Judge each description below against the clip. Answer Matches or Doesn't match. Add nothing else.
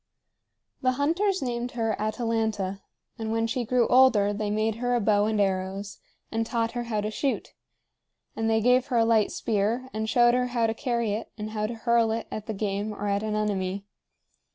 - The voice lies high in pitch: Matches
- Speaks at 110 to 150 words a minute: Doesn't match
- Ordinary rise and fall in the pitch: Doesn't match